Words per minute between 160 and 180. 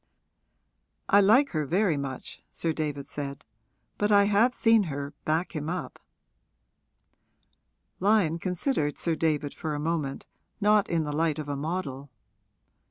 No: average, 140 wpm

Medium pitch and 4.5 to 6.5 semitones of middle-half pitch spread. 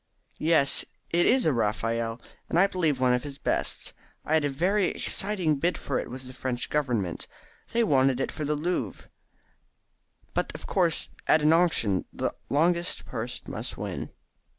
Yes: medium, 150 Hz; average, 5.2 semitones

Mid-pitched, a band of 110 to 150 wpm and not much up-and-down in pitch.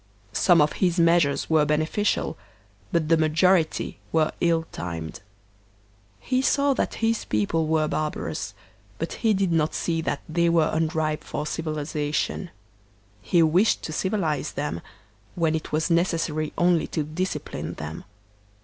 Yes: medium, 160 Hz; average, 140 wpm; narrow, 2.1 semitones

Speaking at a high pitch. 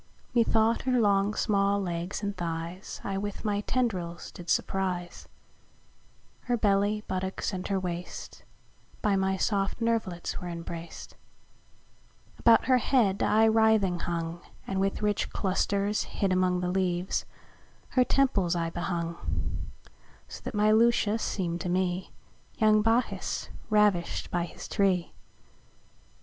Yes: high, 195 Hz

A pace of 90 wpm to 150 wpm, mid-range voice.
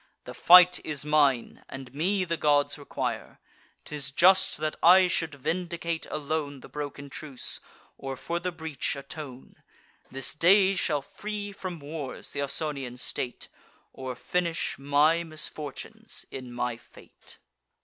Yes: slow, 135 wpm; medium, 150 Hz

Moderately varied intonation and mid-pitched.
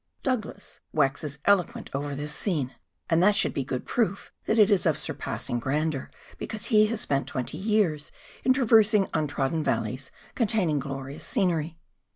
No: wide, 7.1 semitones; medium, 160 Hz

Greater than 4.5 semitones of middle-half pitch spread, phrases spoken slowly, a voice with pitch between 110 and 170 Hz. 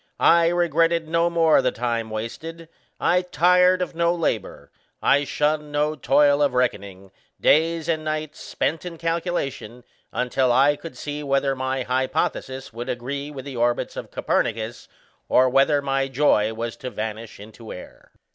No: average, 4.9 semitones; average, 155 wpm; medium, 140 Hz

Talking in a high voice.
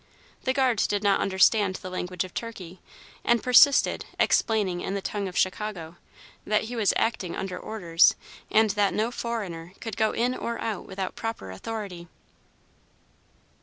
Yes: high, 205 Hz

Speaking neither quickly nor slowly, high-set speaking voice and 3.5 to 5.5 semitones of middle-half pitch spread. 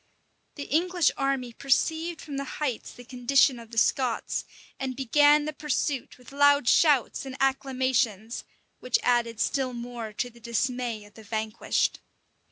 No: average, 150 wpm; very high, 255 Hz; average, 3.0 semitones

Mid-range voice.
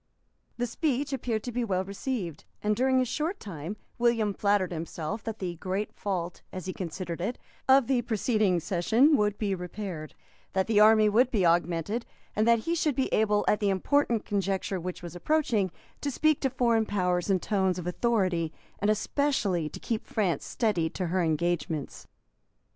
No: high, 205 Hz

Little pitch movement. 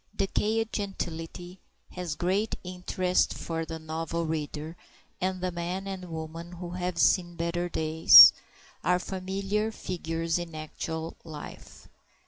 Yes: narrow, 2.2 semitones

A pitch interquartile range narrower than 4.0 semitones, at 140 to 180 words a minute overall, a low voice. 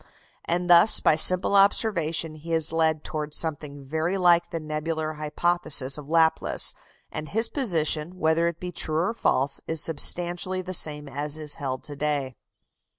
No: narrow, 2.6 semitones; average, 160 wpm; medium, 160 Hz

